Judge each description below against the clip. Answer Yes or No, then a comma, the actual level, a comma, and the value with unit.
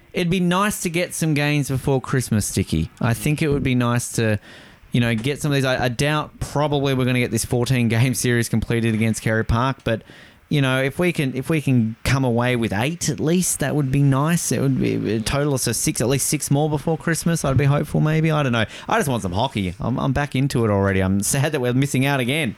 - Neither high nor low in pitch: No, low, 130 Hz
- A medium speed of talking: No, fast, 250 wpm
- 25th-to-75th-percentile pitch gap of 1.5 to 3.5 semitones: No, average, 4.1 semitones